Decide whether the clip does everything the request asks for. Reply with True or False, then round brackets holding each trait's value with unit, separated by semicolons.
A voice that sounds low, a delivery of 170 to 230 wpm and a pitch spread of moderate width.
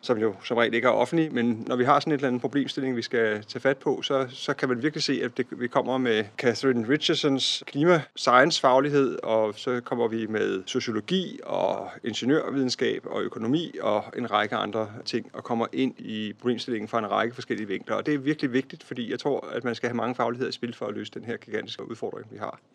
True (125 Hz; 225 wpm; 3.2 semitones)